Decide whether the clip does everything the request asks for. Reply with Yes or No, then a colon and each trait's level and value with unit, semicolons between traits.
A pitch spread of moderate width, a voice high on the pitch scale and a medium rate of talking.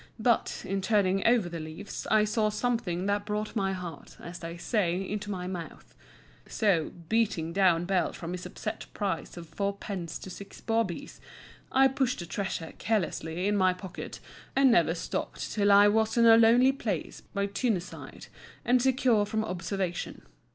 Yes: average, 3.8 semitones; high, 200 Hz; average, 165 wpm